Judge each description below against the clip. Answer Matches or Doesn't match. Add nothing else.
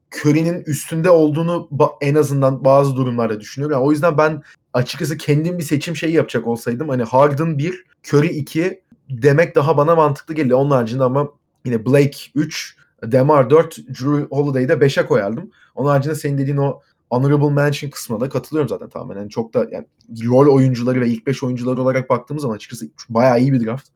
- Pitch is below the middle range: Doesn't match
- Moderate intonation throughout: Matches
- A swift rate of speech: Matches